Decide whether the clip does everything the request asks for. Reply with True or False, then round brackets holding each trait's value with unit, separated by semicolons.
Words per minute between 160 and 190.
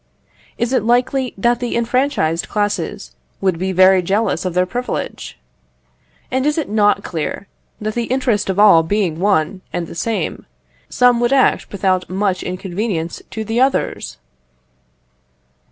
False (145 wpm)